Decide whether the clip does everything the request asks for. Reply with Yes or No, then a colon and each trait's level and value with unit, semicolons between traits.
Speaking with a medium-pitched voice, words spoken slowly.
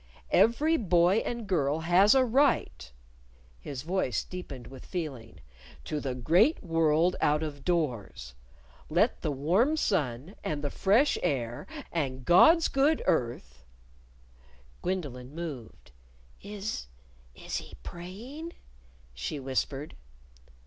Yes: medium, 160 Hz; slow, 115 wpm